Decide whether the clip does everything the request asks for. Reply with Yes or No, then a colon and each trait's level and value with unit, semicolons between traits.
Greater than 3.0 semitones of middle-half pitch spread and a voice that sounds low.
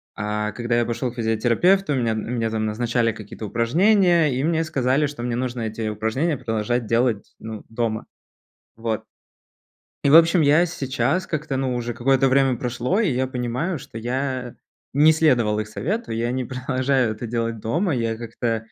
Yes: average, 3.6 semitones; low, 125 Hz